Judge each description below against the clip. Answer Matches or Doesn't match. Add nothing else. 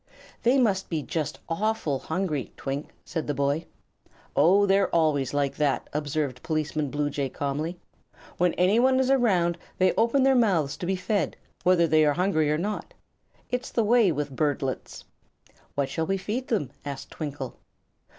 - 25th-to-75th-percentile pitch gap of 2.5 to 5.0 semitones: Doesn't match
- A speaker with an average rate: Matches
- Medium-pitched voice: Matches